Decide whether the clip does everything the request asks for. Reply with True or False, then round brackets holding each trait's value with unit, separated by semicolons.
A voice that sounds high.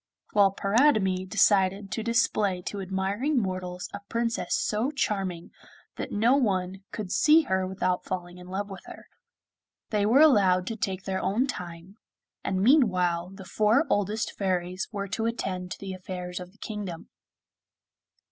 True (195 Hz)